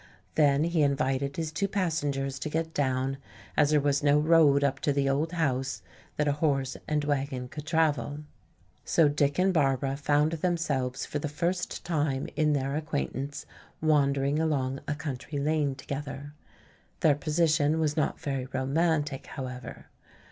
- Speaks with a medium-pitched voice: Yes, medium, 145 Hz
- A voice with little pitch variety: Yes, narrow, 2.2 semitones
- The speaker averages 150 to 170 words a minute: Yes, average, 155 wpm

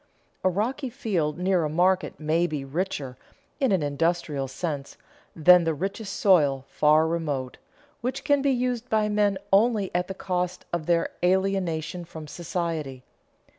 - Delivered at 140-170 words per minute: Yes, average, 150 wpm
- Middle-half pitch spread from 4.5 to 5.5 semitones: No, average, 4.1 semitones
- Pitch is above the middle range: No, medium, 175 Hz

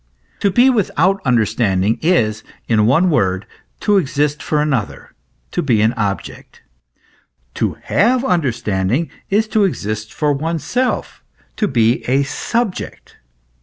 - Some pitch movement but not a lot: No, wide, 9.0 semitones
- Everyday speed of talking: No, slow, 125 wpm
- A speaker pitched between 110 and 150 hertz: Yes, medium, 140 Hz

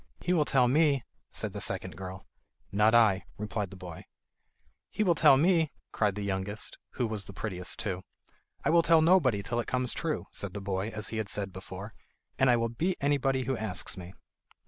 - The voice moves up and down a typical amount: No, wide, 5.7 semitones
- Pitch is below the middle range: Yes, low, 110 Hz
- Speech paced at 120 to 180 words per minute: No, average, 200 wpm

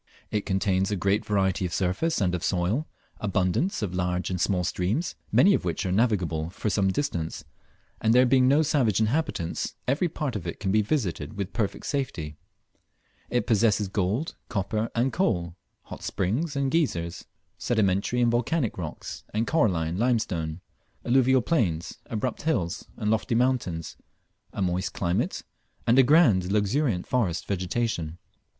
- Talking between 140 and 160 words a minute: Yes, average, 155 wpm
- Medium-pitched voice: No, low, 105 Hz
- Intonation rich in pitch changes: Yes, wide, 5.7 semitones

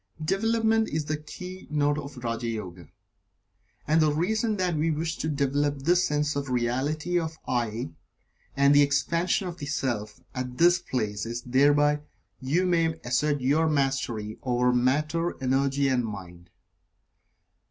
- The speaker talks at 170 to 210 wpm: No, average, 150 wpm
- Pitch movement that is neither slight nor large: Yes, average, 4.5 semitones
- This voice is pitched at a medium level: Yes, medium, 145 Hz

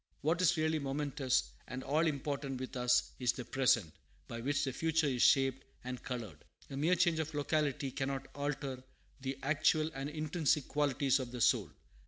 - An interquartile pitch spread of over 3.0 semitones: No, average, 2.7 semitones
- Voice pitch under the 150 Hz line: Yes, medium, 140 Hz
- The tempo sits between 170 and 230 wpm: Yes, average, 175 wpm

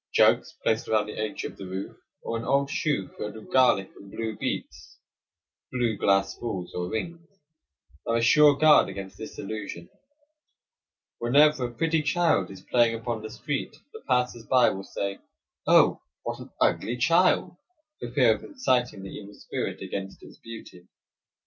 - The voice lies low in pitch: Yes, low, 115 Hz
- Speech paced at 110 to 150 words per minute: No, average, 165 wpm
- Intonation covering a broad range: Yes, wide, 5.8 semitones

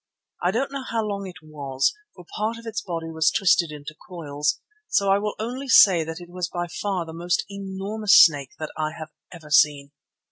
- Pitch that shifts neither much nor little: Yes, average, 4.5 semitones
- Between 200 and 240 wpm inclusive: Yes, fast, 205 wpm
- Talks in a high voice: No, medium, 175 Hz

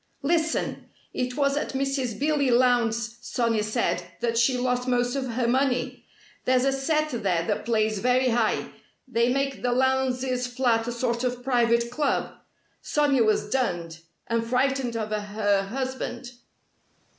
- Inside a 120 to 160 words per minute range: Yes, average, 145 wpm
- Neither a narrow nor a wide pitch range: No, narrow, 2.3 semitones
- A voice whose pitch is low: No, high, 245 Hz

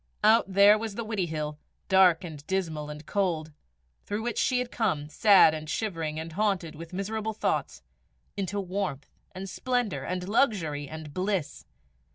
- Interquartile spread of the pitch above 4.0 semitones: Yes, average, 4.9 semitones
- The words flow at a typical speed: Yes, average, 155 wpm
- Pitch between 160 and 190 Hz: Yes, medium, 185 Hz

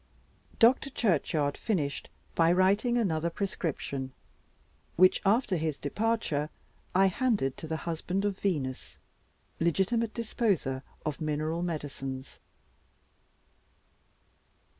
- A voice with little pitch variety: No, wide, 5.4 semitones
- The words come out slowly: Yes, slow, 95 wpm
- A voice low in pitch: No, medium, 170 Hz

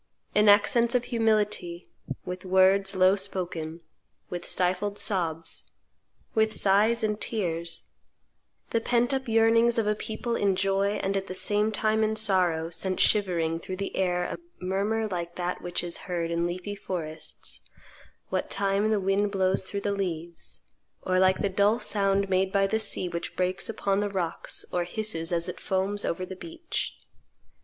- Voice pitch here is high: Yes, high, 195 Hz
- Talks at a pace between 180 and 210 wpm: No, average, 165 wpm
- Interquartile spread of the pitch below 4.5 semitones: Yes, average, 2.9 semitones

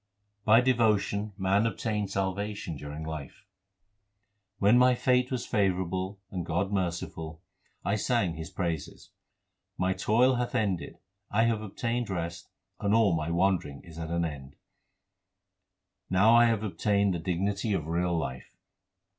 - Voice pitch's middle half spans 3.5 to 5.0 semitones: Yes, average, 4.2 semitones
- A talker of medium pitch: No, very low, 95 Hz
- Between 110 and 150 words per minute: Yes, average, 140 wpm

